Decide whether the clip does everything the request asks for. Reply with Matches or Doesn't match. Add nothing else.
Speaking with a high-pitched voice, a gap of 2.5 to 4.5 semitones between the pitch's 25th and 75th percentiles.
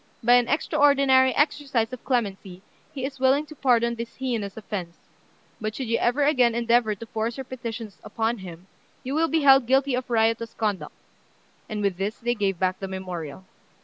Matches